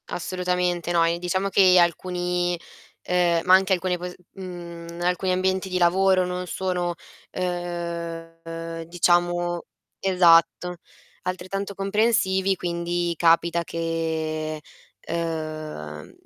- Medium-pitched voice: Yes, medium, 175 Hz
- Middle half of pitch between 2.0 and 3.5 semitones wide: No, narrow, 1.5 semitones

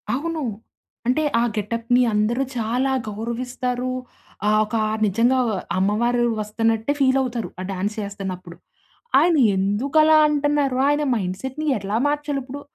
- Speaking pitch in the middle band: No, high, 240 Hz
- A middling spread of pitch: Yes, average, 4.4 semitones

